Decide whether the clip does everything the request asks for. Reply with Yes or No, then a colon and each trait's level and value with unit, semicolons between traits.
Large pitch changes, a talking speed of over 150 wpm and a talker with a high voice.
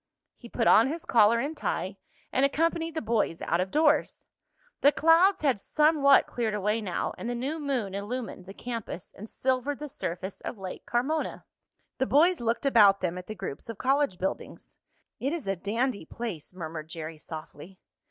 Yes: wide, 6.6 semitones; average, 180 wpm; high, 235 Hz